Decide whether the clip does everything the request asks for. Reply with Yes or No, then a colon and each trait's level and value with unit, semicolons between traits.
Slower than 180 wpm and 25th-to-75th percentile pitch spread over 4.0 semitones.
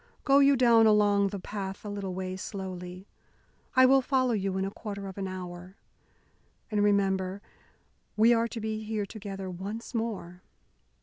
No: average, 165 wpm; average, 2.8 semitones